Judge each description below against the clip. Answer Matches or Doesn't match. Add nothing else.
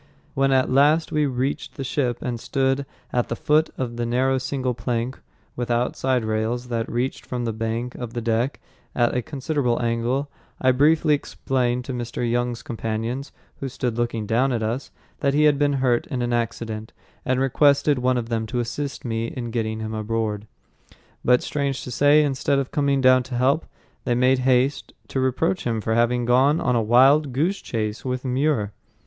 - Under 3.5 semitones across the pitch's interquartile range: Matches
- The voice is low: Matches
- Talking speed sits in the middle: Matches